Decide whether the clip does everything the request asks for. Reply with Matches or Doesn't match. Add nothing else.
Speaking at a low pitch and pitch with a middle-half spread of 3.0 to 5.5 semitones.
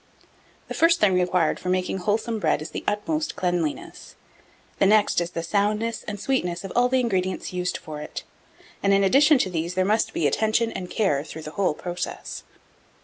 Doesn't match